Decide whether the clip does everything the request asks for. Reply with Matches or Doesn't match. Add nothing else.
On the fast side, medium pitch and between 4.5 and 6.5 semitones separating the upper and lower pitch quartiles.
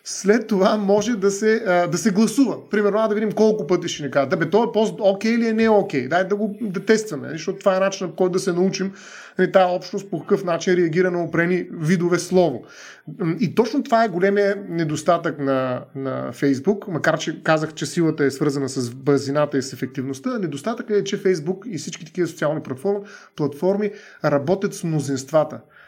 Matches